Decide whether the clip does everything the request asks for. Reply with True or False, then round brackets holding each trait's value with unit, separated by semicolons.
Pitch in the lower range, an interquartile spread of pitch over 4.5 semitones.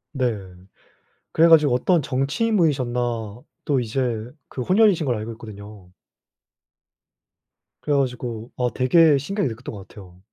True (130 Hz; 5.2 semitones)